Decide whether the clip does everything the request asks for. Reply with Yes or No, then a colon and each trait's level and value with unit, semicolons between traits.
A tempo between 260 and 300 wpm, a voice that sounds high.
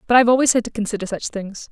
Yes: fast, 280 wpm; high, 225 Hz